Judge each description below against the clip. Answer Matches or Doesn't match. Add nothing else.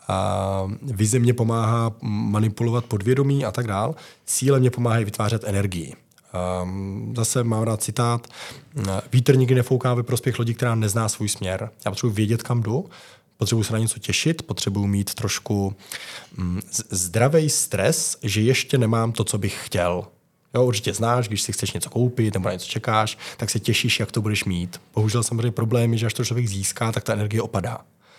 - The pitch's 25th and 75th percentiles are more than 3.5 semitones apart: Doesn't match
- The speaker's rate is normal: Doesn't match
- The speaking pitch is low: Matches